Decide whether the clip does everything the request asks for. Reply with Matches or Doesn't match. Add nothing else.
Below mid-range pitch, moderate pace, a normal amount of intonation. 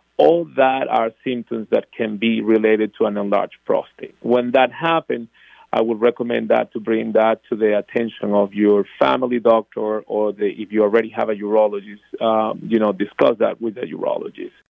Doesn't match